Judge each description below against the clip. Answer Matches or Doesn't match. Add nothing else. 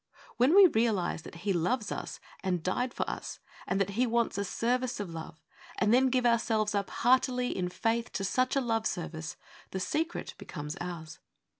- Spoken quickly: Doesn't match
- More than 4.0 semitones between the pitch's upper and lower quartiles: Matches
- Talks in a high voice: Matches